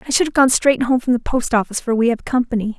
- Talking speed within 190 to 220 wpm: No, fast, 300 wpm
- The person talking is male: No, female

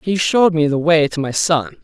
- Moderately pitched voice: Yes, medium, 160 Hz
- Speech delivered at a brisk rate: Yes, fast, 260 wpm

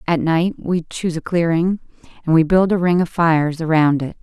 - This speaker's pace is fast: Yes, fast, 215 wpm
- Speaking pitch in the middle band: Yes, medium, 165 Hz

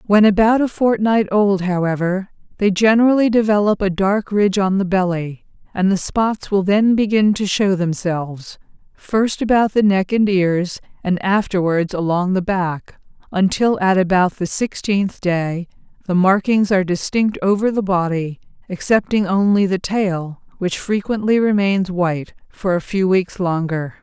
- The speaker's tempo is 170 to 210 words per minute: No, average, 150 wpm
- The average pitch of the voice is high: Yes, high, 195 Hz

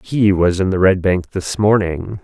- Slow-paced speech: No, fast, 215 wpm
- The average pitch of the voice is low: Yes, very low, 95 Hz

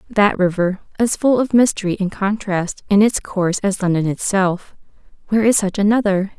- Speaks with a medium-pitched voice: No, high, 200 Hz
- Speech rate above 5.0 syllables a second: Yes, 5.2 syllables/s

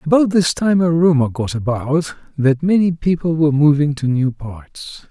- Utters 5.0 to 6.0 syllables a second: No, 4.6 syllables/s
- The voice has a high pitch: No, medium, 150 Hz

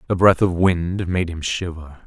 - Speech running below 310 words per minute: Yes, fast, 205 wpm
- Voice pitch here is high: No, very low, 90 Hz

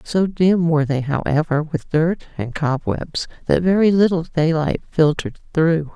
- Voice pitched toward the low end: No, medium, 160 Hz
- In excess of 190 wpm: No, average, 150 wpm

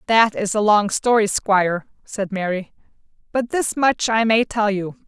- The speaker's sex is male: No, female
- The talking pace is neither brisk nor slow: Yes, average, 175 wpm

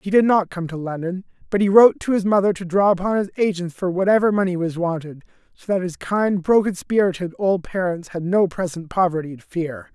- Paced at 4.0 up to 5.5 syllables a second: No, 5.7 syllables/s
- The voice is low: No, medium, 185 Hz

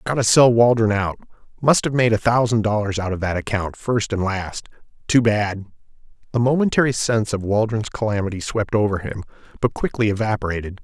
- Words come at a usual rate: Yes, average, 170 wpm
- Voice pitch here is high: No, low, 110 Hz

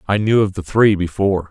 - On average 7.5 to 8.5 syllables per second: No, 5.9 syllables/s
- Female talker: No, male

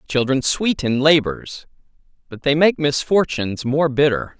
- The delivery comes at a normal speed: No, slow, 125 wpm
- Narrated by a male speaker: Yes, male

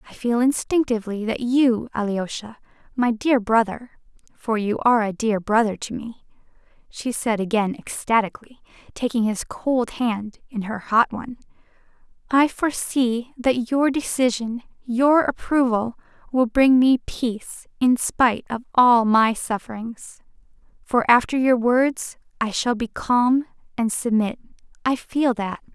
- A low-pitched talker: No, high, 235 Hz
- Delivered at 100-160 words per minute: Yes, slow, 135 wpm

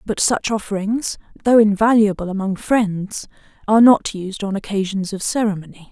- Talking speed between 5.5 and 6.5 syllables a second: No, 5.1 syllables/s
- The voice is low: No, high, 205 Hz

